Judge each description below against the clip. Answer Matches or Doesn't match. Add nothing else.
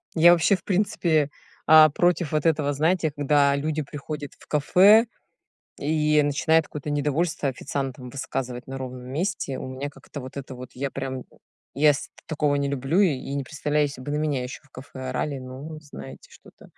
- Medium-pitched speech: Matches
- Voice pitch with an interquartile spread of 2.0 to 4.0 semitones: Matches